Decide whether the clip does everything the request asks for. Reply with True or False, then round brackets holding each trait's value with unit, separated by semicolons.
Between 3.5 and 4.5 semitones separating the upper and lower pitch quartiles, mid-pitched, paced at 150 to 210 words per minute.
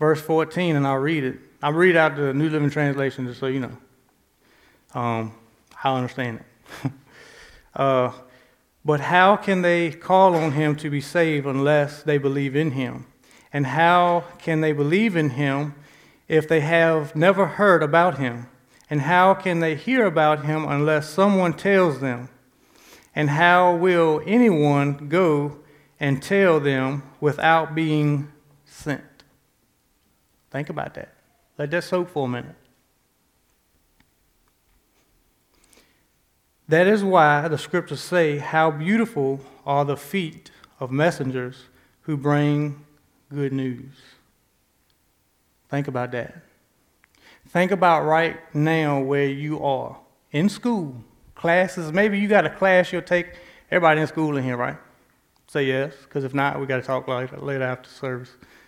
False (3.8 semitones; 150 Hz; 140 wpm)